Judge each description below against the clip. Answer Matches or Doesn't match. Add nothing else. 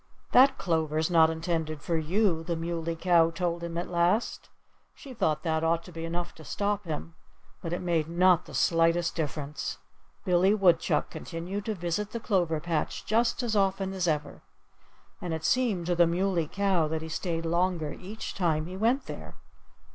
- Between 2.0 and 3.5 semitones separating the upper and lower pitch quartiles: Matches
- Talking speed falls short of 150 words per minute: Doesn't match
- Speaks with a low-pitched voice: Doesn't match